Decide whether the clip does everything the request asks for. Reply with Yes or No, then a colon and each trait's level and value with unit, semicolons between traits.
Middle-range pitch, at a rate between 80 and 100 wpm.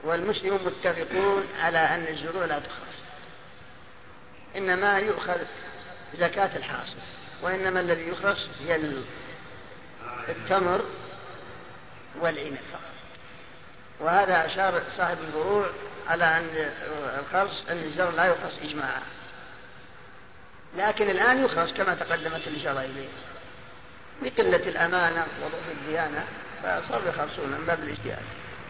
Yes: medium, 170 Hz; average, 90 wpm